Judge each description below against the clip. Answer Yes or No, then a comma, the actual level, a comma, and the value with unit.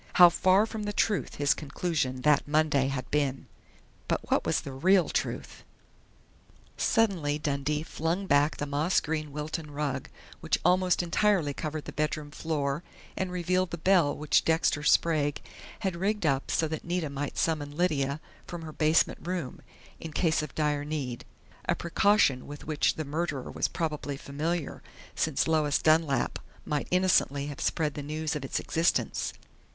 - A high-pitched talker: No, medium, 155 Hz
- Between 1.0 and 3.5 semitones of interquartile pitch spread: Yes, average, 3.0 semitones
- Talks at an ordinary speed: Yes, average, 160 wpm